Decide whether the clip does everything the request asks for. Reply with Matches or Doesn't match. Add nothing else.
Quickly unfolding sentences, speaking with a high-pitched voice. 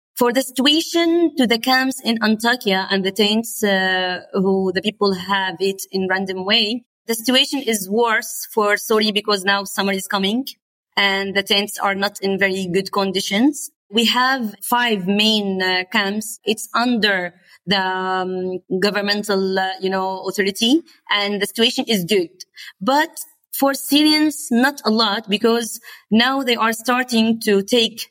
Doesn't match